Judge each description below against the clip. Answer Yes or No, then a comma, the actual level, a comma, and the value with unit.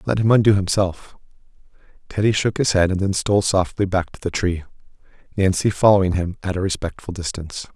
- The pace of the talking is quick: No, average, 180 wpm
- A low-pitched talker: Yes, very low, 95 Hz